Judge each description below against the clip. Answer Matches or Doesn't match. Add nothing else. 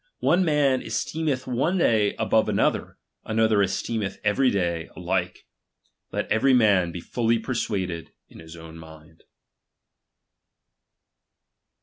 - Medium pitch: Doesn't match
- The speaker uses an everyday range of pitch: Doesn't match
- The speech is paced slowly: Matches